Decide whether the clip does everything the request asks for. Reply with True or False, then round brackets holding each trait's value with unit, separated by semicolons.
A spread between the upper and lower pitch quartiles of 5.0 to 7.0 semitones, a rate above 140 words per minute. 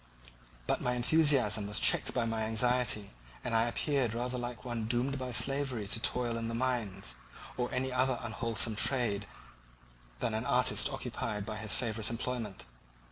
False (2.4 semitones; 160 wpm)